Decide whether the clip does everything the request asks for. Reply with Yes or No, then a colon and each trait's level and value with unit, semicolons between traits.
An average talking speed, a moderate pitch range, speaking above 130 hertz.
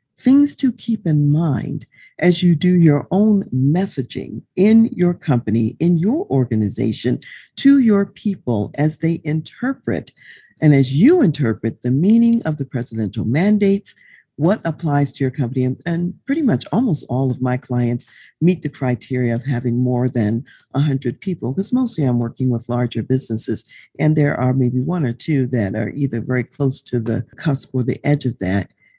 No: average, 170 wpm; wide, 6.2 semitones; medium, 140 Hz